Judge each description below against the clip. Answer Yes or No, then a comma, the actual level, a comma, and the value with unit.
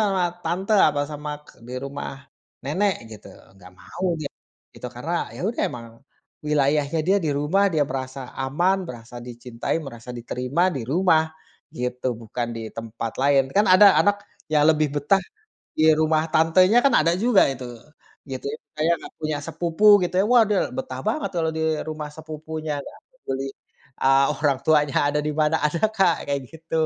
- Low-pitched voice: No, medium, 150 Hz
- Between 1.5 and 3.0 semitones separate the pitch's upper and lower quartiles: No, average, 4.5 semitones